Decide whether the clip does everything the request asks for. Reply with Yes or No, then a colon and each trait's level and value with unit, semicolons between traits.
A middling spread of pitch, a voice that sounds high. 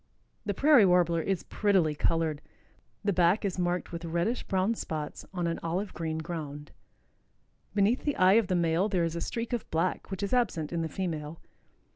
No: average, 3.4 semitones; medium, 175 Hz